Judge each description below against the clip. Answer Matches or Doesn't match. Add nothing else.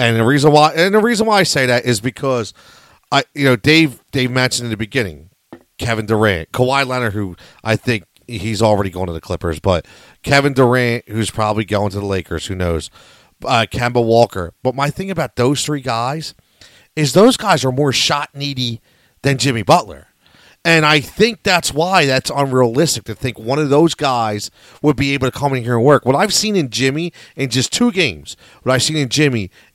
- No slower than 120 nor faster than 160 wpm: Doesn't match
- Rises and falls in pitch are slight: Doesn't match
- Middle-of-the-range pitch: Doesn't match